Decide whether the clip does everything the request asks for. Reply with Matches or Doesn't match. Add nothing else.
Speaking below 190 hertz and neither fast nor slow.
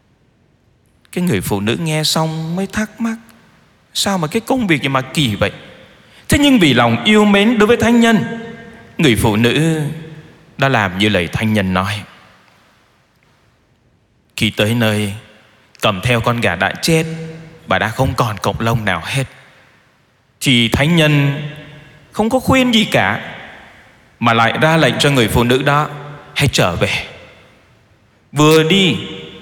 Doesn't match